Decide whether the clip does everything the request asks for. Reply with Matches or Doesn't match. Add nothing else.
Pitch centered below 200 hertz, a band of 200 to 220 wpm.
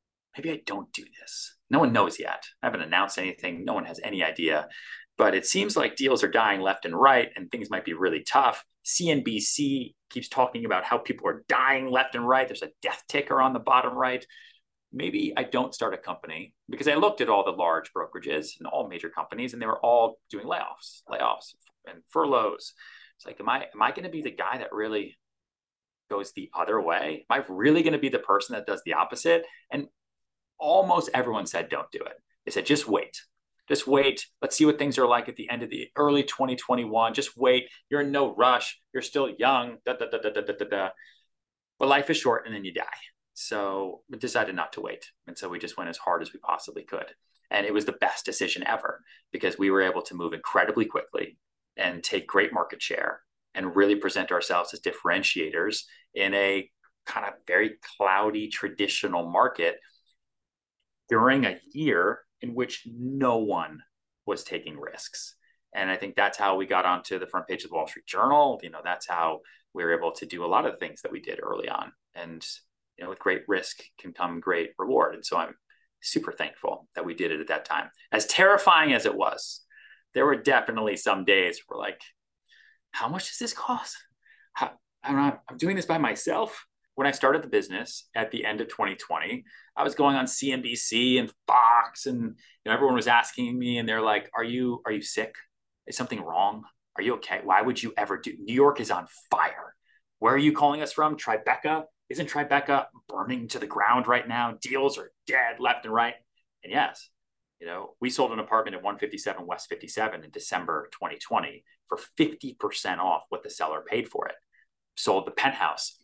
Matches